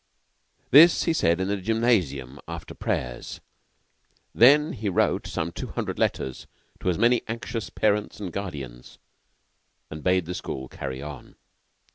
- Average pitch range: No, wide, 7.6 semitones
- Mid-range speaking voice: No, very low, 95 Hz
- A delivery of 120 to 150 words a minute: Yes, average, 140 wpm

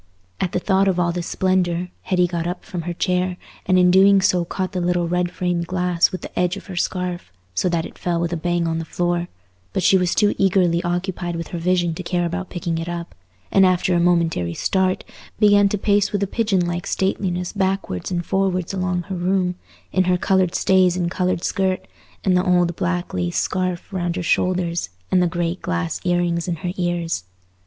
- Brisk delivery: Yes, fast, 215 wpm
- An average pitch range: No, narrow, 1.3 semitones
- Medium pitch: Yes, medium, 180 Hz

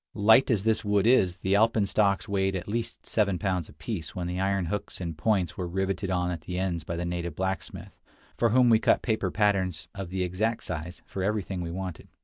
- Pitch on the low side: Yes, very low, 95 Hz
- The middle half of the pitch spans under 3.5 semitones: Yes, average, 2.8 semitones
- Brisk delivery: Yes, fast, 210 wpm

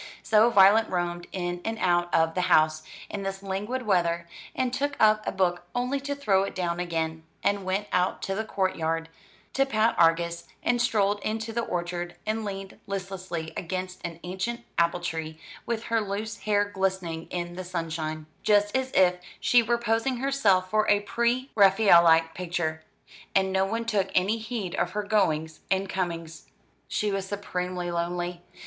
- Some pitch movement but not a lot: Yes, average, 3.7 semitones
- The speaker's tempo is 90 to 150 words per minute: No, average, 170 wpm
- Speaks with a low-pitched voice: No, high, 190 Hz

